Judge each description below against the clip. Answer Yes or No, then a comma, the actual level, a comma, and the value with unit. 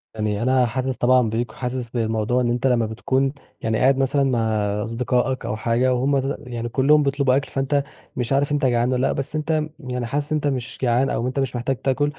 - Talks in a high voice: No, low, 130 Hz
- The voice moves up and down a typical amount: No, narrow, 2.3 semitones